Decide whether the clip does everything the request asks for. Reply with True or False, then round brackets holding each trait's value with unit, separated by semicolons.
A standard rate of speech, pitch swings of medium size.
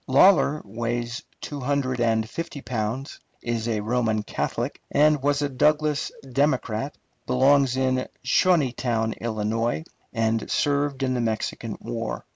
False (125 wpm; 3.8 semitones)